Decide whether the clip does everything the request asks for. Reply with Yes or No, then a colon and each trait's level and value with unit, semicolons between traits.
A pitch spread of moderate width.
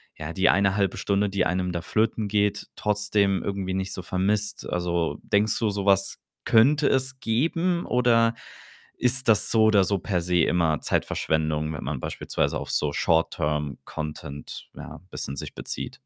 Yes: average, 4.4 semitones